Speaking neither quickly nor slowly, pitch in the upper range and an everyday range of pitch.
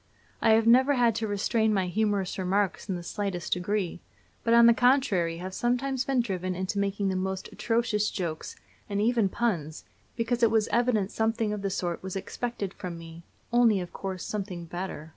Yes: average, 185 wpm; high, 205 Hz; average, 3.8 semitones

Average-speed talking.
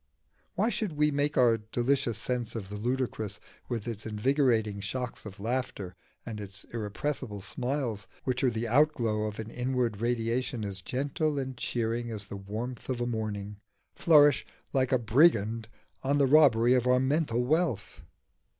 Yes: average, 155 wpm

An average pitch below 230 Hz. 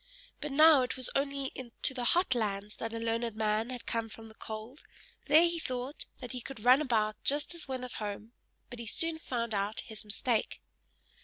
No: high, 245 Hz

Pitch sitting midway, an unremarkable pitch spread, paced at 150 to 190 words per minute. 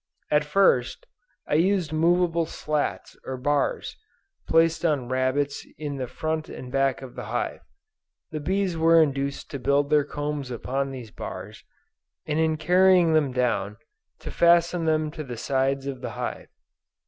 Yes: medium, 150 Hz; average, 3.3 semitones; average, 155 wpm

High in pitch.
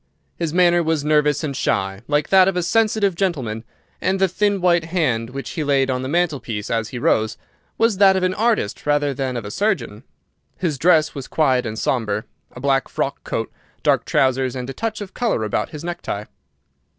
No: medium, 150 Hz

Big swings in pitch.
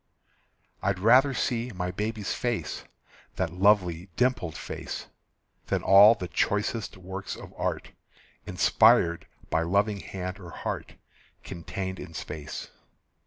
No: average, 3.0 semitones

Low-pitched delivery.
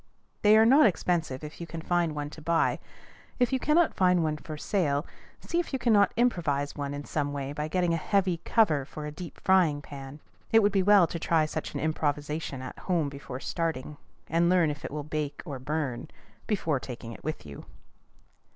No: medium, 155 Hz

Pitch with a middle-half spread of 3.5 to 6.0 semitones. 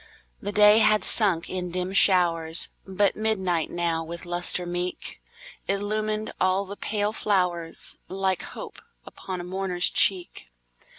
No: narrow, 2.6 semitones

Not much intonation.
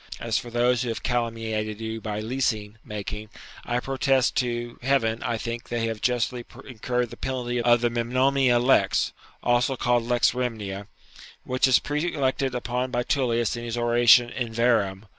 Yes: narrow, 1.8 semitones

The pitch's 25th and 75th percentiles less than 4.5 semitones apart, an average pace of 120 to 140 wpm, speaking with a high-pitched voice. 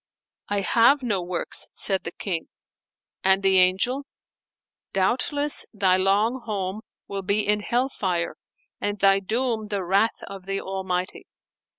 Yes: average, 2.8 semitones; slow, 135 wpm; high, 195 Hz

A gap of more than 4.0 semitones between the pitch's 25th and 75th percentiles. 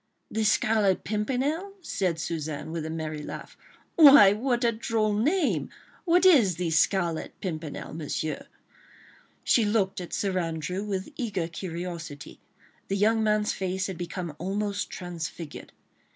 Yes: average, 4.7 semitones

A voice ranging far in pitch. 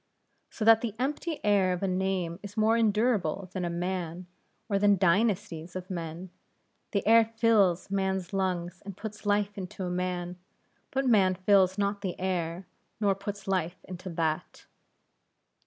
No: narrow, 2.4 semitones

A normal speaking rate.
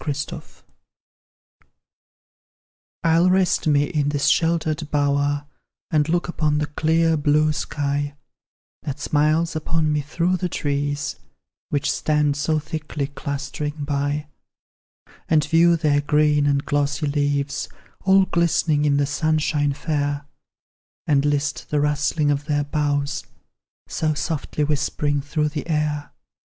No: slow, 125 wpm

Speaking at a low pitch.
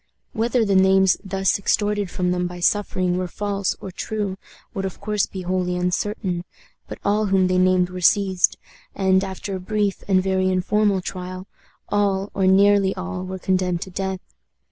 No: high, 190 Hz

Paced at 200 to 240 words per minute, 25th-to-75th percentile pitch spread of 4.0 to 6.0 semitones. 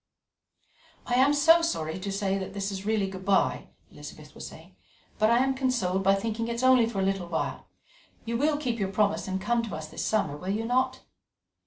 Yes: fast, 205 wpm; average, 4.4 semitones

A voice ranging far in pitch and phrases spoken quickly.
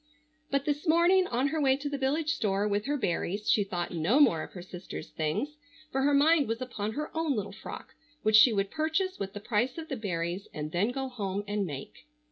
Yes: wide, 6.6 semitones; fast, 225 wpm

